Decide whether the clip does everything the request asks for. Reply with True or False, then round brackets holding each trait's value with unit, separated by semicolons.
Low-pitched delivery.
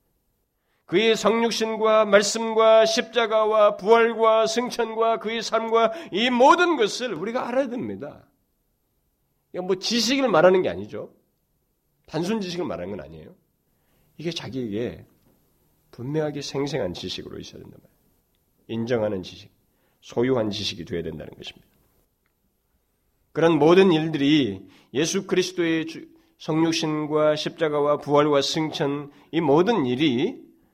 False (180 Hz)